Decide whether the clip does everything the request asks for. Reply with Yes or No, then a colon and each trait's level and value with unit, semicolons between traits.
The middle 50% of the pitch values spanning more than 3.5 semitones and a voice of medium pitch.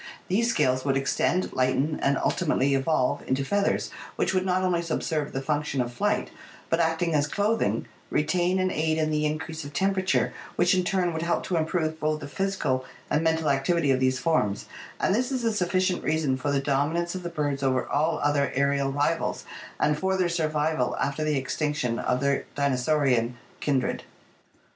Yes: average, 3.9 semitones; medium, 155 Hz